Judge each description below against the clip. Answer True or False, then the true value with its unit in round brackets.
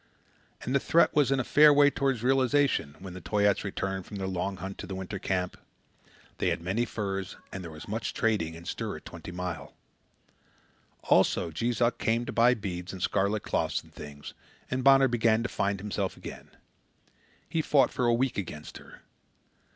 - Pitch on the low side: True (105 Hz)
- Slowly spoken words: False (190 wpm)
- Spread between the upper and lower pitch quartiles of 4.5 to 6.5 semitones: True (4.9 semitones)